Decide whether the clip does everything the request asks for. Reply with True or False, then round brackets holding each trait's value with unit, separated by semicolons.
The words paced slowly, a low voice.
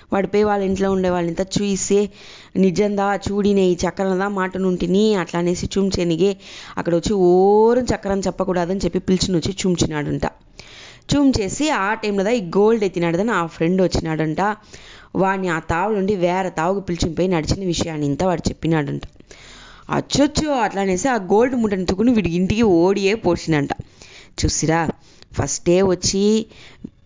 False (130 wpm; 190 Hz)